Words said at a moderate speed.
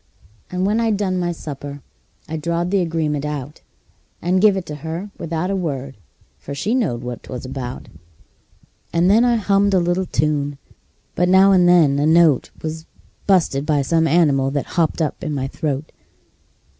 Yes: average, 175 wpm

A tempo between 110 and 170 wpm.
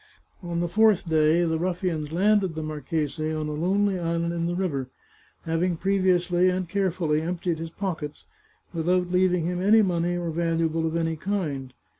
Yes: average, 165 wpm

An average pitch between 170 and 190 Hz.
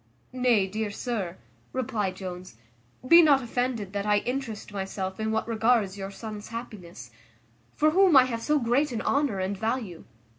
No: high, 220 Hz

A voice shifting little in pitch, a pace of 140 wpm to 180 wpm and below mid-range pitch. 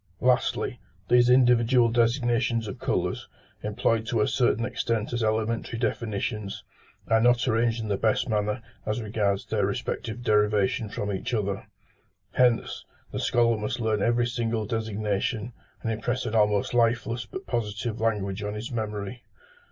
Yes: narrow, 2.1 semitones; average, 145 wpm; low, 115 Hz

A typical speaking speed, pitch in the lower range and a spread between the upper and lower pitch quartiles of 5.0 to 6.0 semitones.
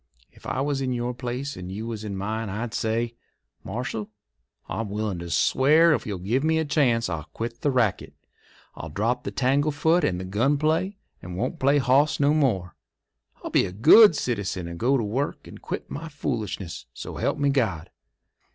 Yes: average, 190 wpm; low, 120 Hz; wide, 5.6 semitones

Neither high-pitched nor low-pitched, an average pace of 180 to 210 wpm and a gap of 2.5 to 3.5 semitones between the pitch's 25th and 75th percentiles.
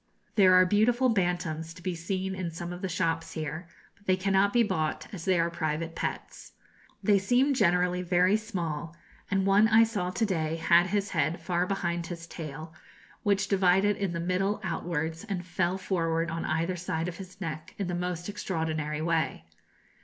Yes: medium, 180 Hz; average, 185 wpm; average, 2.8 semitones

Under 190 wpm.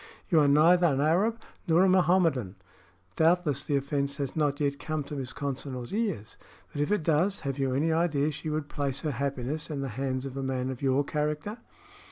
No: fast, 205 wpm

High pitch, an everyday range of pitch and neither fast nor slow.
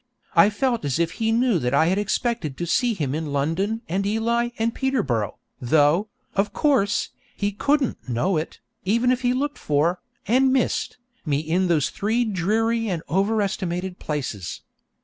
No: high, 195 Hz; wide, 6.5 semitones; average, 170 wpm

